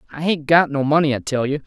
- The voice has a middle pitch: Yes, medium, 145 Hz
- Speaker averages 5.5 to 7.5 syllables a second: Yes, 6.5 syllables/s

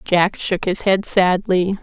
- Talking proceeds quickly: No, average, 165 wpm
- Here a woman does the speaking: Yes, female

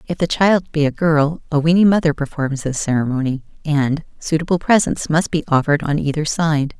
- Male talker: No, female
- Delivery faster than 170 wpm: Yes, average, 185 wpm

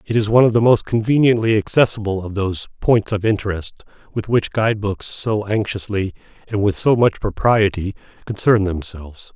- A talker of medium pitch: No, low, 105 Hz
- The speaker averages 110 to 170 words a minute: Yes, average, 165 wpm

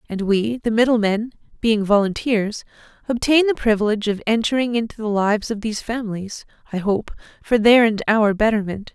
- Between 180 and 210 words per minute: No, average, 160 wpm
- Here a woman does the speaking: Yes, female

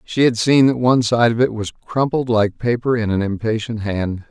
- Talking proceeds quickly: Yes, fast, 225 wpm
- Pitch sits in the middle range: No, low, 115 Hz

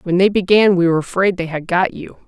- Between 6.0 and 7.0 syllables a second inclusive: Yes, 6.2 syllables/s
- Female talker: Yes, female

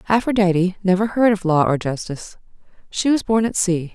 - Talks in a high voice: Yes, high, 195 Hz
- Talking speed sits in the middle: Yes, average, 185 wpm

